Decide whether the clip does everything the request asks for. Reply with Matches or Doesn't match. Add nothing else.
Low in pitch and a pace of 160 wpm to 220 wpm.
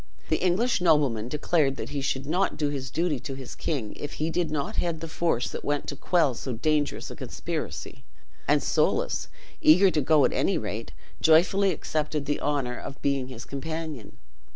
Doesn't match